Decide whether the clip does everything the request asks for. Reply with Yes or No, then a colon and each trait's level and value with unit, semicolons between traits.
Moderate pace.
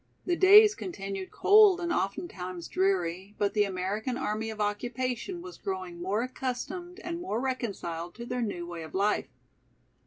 Yes: average, 155 wpm